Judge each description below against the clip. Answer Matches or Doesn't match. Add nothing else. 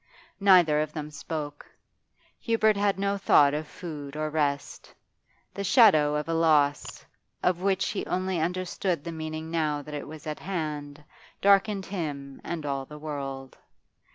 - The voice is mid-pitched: Matches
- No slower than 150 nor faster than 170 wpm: Matches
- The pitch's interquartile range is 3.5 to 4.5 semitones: Matches